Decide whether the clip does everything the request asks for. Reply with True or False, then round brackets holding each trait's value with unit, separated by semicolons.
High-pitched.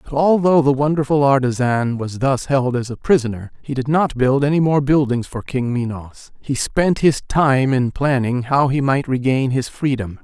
False (135 Hz)